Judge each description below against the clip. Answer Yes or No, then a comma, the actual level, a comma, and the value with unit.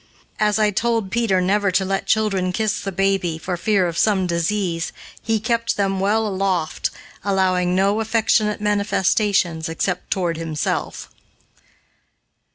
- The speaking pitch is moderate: No, high, 195 Hz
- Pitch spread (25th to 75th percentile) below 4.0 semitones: Yes, narrow, 2.6 semitones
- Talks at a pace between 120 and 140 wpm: Yes, slow, 135 wpm